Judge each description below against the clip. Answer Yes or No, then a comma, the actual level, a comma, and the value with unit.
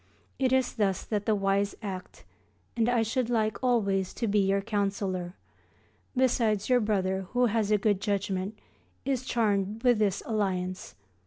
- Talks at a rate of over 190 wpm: No, average, 155 wpm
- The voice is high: Yes, high, 210 Hz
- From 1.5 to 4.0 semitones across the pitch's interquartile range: Yes, average, 2.9 semitones